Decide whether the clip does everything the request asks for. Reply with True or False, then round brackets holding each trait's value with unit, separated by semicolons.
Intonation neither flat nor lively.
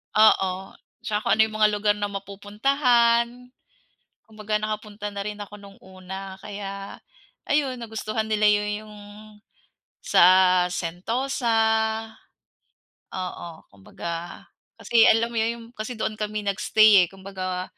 False (2.1 semitones)